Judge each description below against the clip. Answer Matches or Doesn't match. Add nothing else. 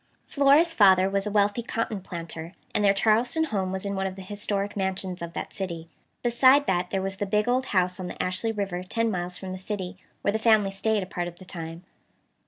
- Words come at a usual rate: Doesn't match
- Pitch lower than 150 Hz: Doesn't match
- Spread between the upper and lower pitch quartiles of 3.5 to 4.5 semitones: Doesn't match